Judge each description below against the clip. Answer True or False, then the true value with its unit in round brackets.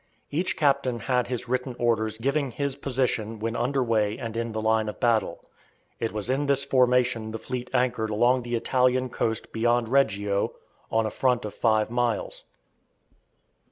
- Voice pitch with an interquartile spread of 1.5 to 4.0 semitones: True (2.5 semitones)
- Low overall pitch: True (120 Hz)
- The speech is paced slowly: False (165 wpm)